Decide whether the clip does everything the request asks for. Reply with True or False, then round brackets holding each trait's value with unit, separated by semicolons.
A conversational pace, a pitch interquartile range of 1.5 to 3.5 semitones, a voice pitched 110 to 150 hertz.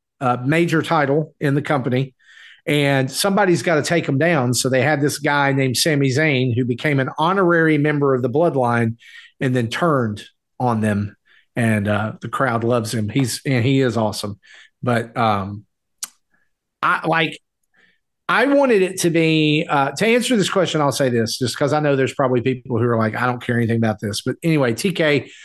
False (195 wpm; 4.4 semitones; 135 Hz)